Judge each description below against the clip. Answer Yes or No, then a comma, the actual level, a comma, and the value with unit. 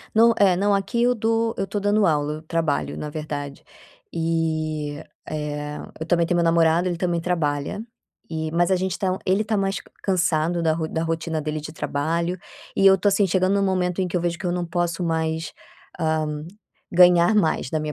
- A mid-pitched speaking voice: Yes, medium, 170 Hz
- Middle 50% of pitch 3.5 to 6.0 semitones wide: No, average, 3.1 semitones